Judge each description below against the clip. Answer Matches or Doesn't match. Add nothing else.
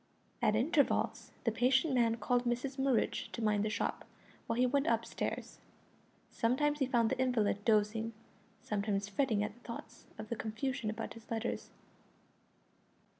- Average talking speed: Matches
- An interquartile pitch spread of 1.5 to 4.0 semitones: Matches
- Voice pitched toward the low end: Doesn't match